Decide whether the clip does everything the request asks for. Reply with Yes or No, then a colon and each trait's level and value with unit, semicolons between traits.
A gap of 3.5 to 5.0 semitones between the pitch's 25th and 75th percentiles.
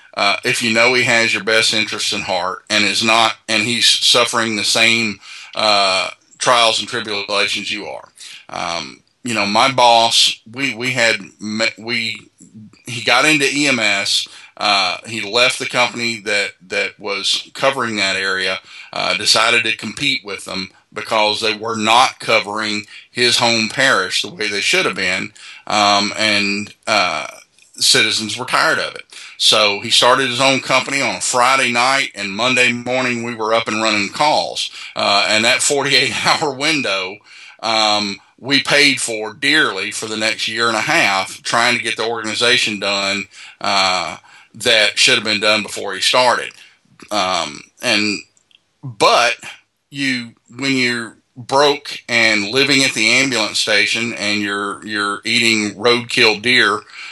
No: average, 2.9 semitones